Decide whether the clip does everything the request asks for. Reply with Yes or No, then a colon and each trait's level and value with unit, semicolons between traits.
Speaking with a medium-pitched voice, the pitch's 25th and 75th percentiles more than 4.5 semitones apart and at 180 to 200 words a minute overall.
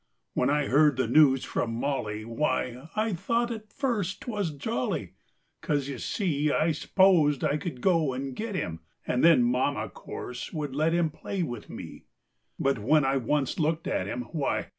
Yes: medium, 150 Hz; average, 5.0 semitones; average, 185 wpm